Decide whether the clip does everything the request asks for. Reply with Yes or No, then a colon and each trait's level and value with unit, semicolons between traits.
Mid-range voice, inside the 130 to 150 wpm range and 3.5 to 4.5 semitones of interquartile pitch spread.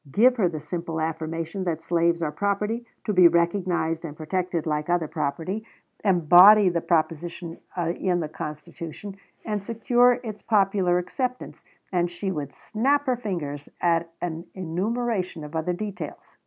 Yes: medium, 175 Hz; average, 145 wpm; average, 3.8 semitones